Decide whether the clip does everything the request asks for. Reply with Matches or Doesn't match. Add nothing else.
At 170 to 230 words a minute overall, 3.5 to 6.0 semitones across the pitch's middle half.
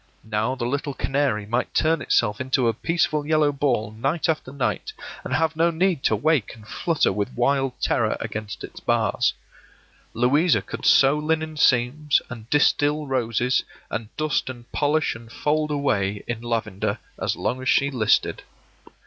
Doesn't match